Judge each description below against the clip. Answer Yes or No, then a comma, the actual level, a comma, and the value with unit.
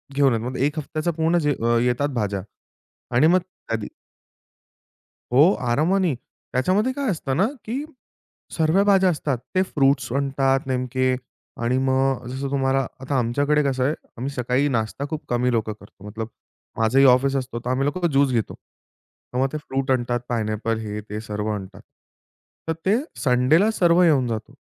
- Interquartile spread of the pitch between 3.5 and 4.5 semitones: Yes, average, 3.9 semitones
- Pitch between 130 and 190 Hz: Yes, low, 135 Hz